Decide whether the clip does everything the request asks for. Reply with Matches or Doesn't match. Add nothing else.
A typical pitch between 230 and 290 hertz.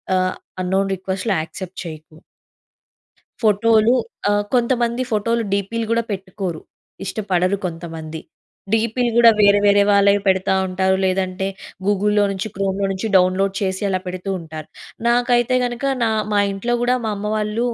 Doesn't match